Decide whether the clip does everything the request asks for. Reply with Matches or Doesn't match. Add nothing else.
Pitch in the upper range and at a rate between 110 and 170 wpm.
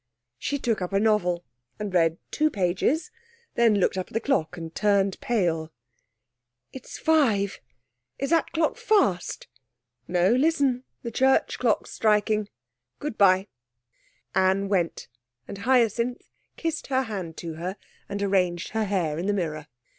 Matches